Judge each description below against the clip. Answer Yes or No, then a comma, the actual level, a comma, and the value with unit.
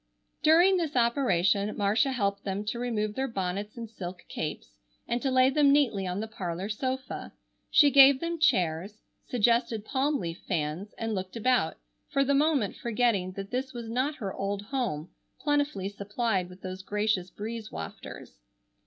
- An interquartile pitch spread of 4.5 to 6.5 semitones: Yes, average, 5.2 semitones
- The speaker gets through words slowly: No, average, 160 wpm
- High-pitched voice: Yes, high, 220 Hz